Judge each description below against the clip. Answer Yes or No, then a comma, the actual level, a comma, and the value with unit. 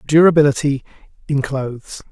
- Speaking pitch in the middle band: Yes, medium, 145 Hz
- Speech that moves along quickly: No, slow, 85 wpm